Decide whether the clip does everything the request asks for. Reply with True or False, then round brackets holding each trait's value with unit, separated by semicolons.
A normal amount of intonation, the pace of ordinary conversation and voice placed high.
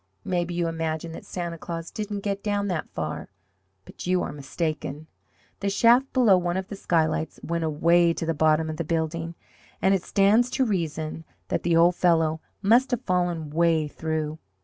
False (3.3 semitones; 180 wpm; 170 Hz)